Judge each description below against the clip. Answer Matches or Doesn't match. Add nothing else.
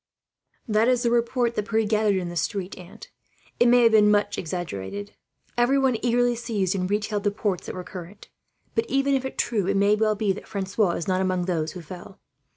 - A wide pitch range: Doesn't match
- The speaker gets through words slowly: Doesn't match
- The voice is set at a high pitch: Matches